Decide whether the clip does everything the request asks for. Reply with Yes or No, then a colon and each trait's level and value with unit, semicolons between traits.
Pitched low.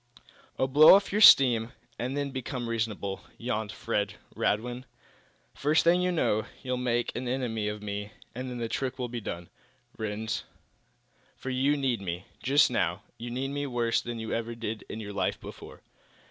Yes: low, 120 Hz